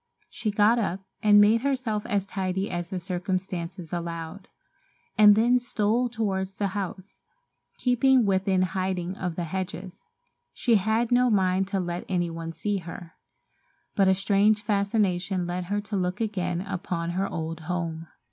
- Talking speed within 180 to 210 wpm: No, average, 155 wpm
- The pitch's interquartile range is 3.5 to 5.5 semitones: No, average, 2.8 semitones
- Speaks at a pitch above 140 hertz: Yes, high, 190 Hz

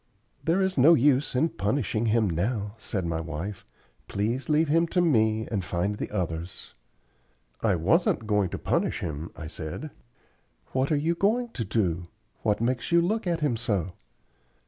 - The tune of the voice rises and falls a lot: Yes, wide, 8.4 semitones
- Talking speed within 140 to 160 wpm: No, average, 170 wpm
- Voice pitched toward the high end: No, low, 110 Hz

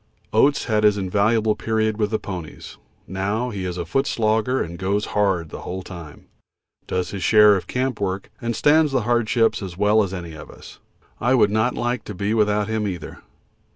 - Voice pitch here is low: Yes, low, 105 Hz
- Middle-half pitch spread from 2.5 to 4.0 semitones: Yes, average, 3.1 semitones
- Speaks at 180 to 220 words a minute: Yes, average, 195 wpm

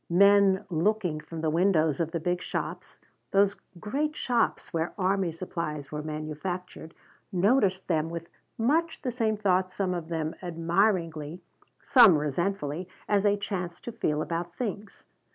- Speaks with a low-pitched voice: No, medium, 180 Hz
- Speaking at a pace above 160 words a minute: No, average, 145 wpm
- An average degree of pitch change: Yes, average, 3.8 semitones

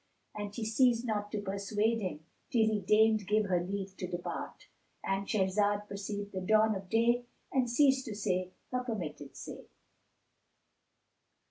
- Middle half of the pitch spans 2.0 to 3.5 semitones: Yes, narrow, 2.5 semitones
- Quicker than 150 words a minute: No, average, 145 wpm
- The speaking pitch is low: No, high, 205 Hz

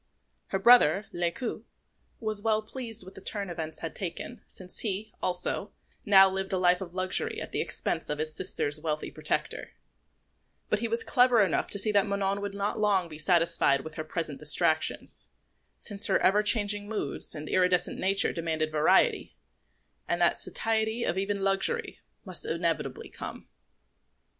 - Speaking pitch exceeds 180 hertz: Yes, high, 190 Hz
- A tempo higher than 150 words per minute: Yes, average, 160 wpm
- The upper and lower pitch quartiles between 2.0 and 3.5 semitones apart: No, average, 3.9 semitones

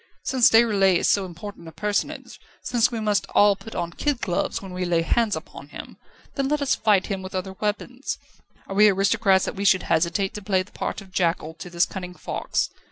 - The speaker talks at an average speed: No, fast, 220 wpm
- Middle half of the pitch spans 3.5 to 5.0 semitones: No, average, 3.0 semitones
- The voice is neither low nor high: No, high, 195 Hz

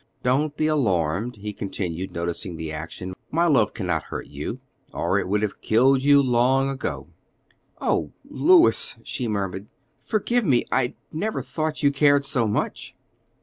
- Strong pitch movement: Yes, wide, 6.9 semitones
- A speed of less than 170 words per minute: Yes, average, 155 wpm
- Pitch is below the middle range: Yes, low, 125 Hz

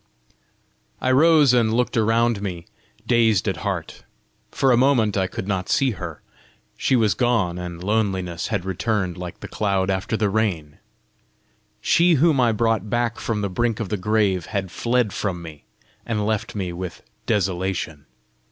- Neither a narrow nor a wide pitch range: Yes, average, 4.0 semitones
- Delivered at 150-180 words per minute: Yes, average, 160 wpm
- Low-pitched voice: Yes, low, 105 Hz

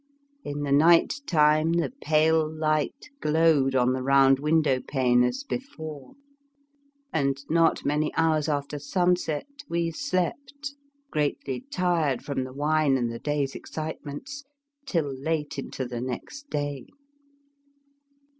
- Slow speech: Yes, slow, 125 wpm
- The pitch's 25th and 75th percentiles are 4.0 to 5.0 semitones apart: No, average, 3.0 semitones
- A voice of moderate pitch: Yes, medium, 150 Hz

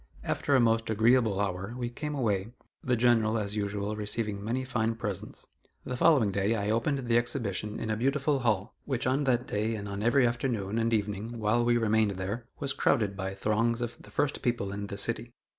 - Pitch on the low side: Yes, low, 115 Hz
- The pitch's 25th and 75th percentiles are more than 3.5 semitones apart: No, average, 2.8 semitones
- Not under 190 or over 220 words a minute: Yes, average, 200 wpm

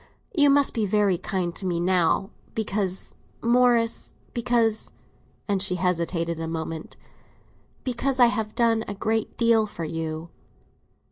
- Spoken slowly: Yes, slow, 125 wpm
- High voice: Yes, high, 205 Hz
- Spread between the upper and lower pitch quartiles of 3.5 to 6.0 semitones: Yes, average, 5.1 semitones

